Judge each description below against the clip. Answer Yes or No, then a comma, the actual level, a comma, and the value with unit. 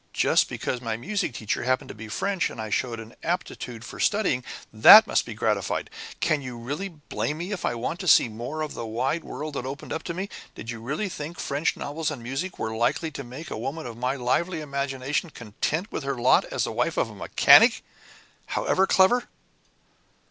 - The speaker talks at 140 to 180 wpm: No, fast, 205 wpm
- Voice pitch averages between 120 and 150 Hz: Yes, medium, 140 Hz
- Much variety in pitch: Yes, wide, 5.8 semitones